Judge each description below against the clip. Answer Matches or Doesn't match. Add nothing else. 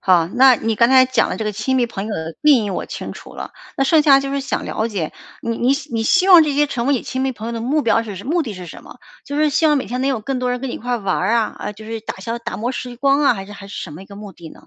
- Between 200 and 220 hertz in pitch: Doesn't match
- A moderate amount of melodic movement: Matches